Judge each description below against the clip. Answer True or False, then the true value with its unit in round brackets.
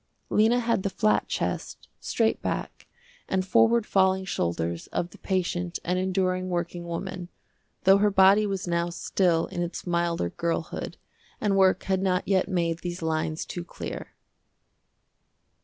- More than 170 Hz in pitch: True (185 Hz)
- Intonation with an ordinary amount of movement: False (2.0 semitones)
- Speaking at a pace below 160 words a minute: True (145 wpm)